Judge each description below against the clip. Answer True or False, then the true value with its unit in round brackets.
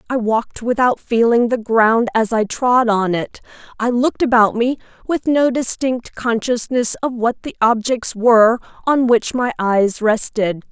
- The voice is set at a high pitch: True (235 Hz)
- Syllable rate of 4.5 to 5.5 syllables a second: False (4.3 syllables/s)